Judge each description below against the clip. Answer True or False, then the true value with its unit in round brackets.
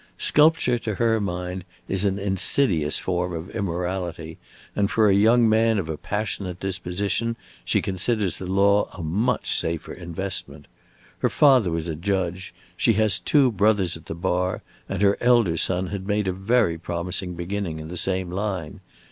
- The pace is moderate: True (165 wpm)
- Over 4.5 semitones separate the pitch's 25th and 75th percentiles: False (3.0 semitones)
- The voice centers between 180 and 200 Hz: False (95 Hz)